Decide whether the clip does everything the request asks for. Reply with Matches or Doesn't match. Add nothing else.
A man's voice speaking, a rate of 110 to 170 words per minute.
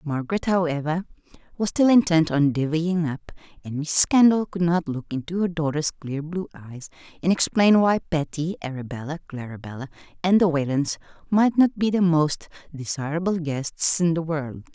Doesn't match